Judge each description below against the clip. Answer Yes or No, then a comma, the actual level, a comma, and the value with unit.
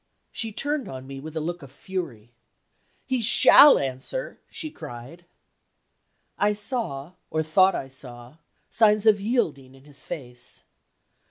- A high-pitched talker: No, medium, 160 Hz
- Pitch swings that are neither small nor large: No, wide, 7.8 semitones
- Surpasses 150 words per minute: No, average, 140 wpm